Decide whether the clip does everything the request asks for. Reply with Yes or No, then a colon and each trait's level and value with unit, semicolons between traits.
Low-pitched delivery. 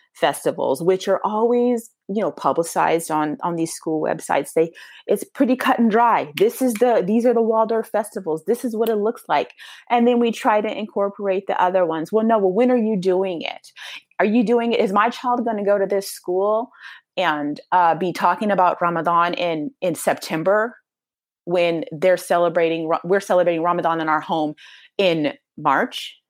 No: high, 200 Hz